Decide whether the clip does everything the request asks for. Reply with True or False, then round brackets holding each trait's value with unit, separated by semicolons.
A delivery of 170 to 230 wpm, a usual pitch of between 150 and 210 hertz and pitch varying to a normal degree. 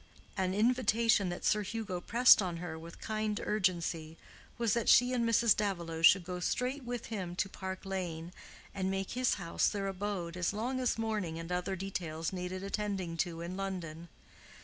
True (175 wpm; 190 Hz; 3.6 semitones)